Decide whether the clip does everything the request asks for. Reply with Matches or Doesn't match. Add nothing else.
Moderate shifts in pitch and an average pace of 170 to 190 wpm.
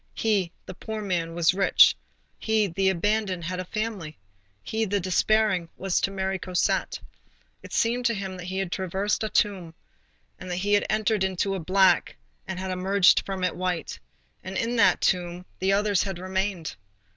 Doesn't match